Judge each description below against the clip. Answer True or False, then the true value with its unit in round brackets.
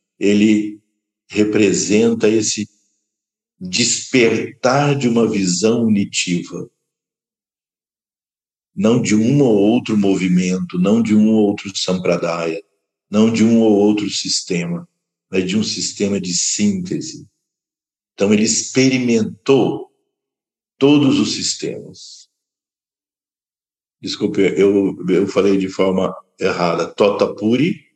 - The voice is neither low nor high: False (105 Hz)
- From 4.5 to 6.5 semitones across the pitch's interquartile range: False (3.5 semitones)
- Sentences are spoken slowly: True (100 wpm)